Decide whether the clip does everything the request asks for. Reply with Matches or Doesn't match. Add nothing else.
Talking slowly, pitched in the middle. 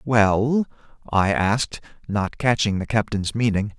Doesn't match